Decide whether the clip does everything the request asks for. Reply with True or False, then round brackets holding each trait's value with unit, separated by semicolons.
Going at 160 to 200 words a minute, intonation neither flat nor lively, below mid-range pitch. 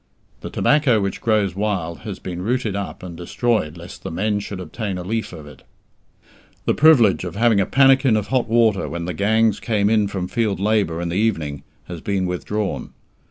True (195 wpm; 3.8 semitones; 100 Hz)